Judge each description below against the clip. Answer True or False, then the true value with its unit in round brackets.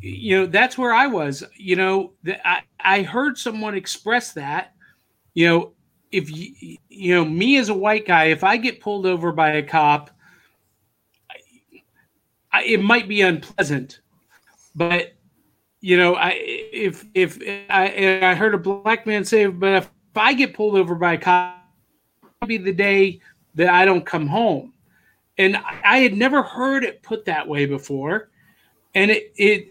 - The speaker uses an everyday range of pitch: True (3.4 semitones)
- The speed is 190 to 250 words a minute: False (175 wpm)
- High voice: True (195 Hz)